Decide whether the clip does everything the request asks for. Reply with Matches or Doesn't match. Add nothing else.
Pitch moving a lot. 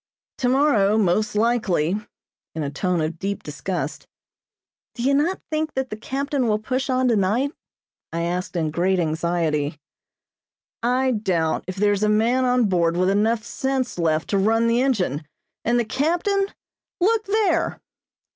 Matches